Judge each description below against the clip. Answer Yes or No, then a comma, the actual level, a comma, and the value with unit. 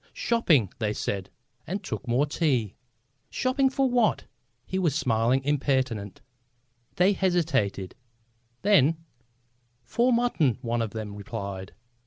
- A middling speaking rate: No, slow, 115 wpm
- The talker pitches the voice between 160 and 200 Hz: No, low, 135 Hz